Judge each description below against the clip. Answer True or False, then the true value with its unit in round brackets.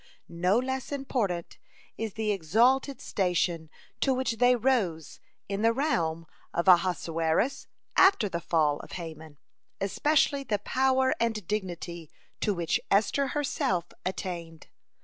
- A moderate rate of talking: False (125 wpm)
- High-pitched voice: True (200 Hz)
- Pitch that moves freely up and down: True (7.1 semitones)